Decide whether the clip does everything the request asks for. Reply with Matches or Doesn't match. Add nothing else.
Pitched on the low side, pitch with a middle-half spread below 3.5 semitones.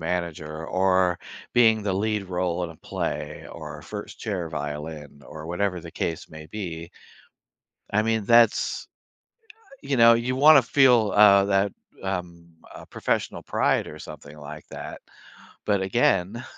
Doesn't match